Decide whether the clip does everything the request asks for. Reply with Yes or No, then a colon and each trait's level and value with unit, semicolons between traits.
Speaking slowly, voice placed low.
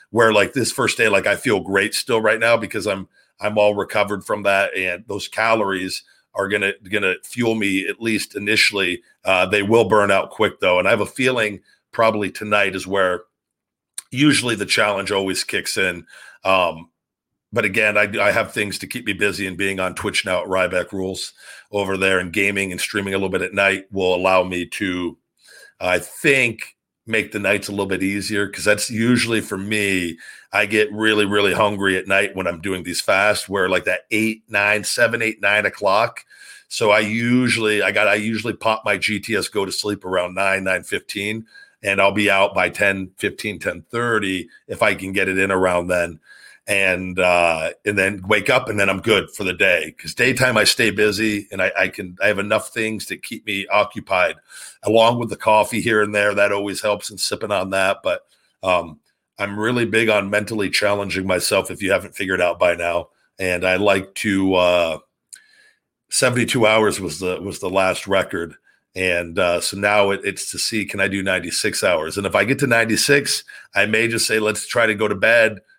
No: fast, 205 wpm; low, 100 Hz